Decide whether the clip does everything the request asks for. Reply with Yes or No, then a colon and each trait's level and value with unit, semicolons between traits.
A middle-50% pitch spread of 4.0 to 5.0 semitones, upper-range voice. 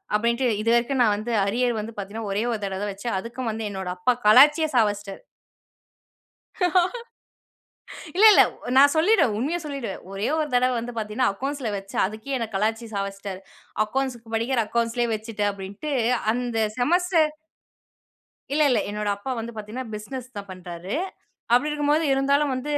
Yes: average, 4.4 semitones; high, 230 Hz